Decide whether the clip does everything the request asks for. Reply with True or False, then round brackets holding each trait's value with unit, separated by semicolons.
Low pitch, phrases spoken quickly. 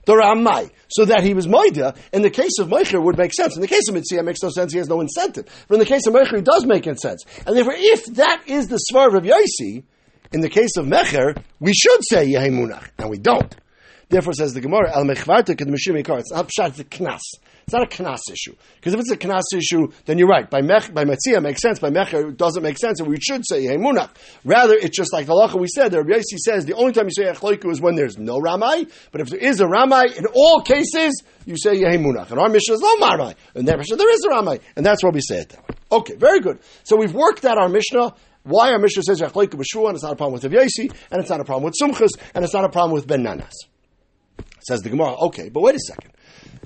False (195 Hz; 255 wpm)